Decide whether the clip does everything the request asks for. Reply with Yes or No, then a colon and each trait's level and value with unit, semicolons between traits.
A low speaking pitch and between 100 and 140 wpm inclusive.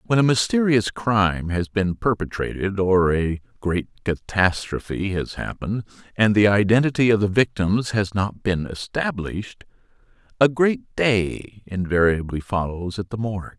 Yes: low, 100 Hz; slow, 135 wpm